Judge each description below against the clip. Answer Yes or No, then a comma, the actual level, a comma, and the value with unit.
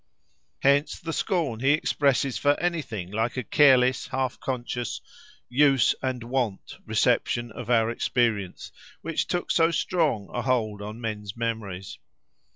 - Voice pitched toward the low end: Yes, low, 125 Hz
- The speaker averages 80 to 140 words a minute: Yes, slow, 135 wpm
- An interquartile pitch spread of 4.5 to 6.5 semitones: No, average, 4.1 semitones